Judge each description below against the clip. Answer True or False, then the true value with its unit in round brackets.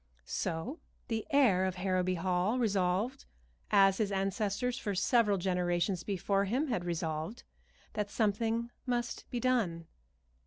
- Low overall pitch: False (200 Hz)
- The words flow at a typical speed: False (125 wpm)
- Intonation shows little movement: False (4.3 semitones)